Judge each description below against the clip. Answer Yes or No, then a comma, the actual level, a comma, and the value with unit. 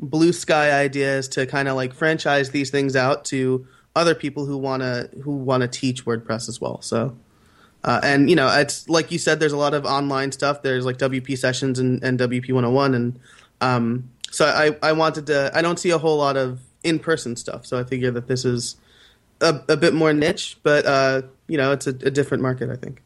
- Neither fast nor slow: No, fast, 220 wpm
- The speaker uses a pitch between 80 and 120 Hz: No, low, 135 Hz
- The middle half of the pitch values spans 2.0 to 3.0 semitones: Yes, narrow, 2.5 semitones